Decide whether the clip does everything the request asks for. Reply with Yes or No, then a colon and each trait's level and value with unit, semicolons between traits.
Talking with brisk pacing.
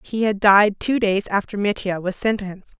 No: average, 195 wpm